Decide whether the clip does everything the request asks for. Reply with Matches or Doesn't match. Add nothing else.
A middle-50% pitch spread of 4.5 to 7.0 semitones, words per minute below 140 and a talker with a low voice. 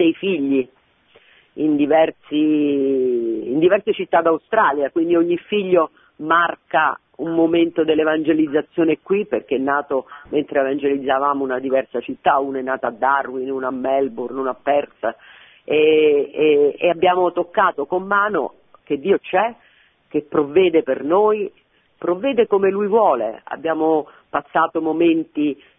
Doesn't match